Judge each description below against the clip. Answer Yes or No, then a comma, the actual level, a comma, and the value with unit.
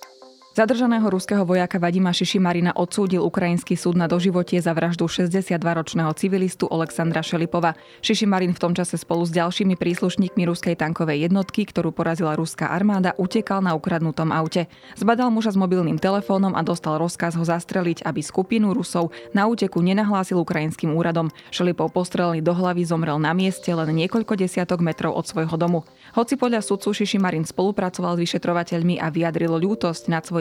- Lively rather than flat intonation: No, narrow, 2.4 semitones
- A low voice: No, medium, 175 Hz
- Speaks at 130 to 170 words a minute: Yes, average, 150 wpm